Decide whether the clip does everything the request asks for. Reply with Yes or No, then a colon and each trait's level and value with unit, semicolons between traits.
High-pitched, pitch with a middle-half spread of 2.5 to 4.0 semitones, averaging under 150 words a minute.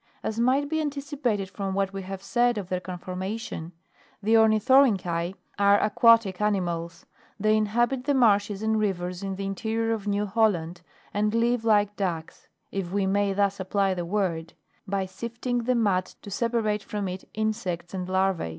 No: high, 205 Hz; average, 3.1 semitones; average, 170 wpm